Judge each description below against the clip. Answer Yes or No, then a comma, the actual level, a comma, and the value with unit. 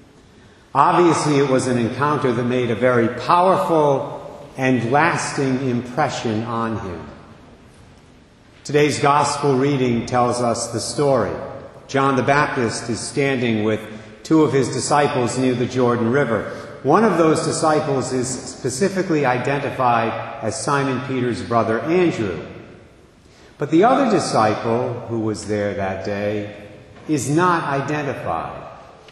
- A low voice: Yes, low, 130 Hz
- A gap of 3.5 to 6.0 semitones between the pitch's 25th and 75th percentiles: Yes, average, 3.9 semitones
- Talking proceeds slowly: Yes, slow, 125 wpm